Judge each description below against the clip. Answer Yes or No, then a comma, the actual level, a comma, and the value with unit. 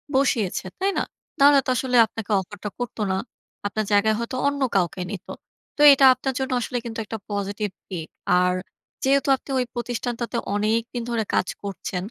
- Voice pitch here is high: Yes, high, 230 Hz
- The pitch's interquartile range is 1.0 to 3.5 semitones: No, average, 4.0 semitones